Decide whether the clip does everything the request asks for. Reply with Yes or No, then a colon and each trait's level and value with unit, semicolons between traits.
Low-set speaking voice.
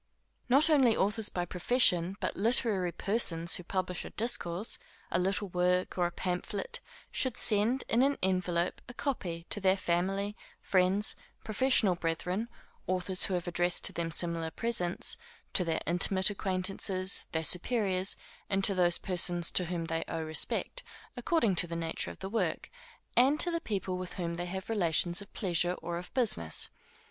No: medium, 185 Hz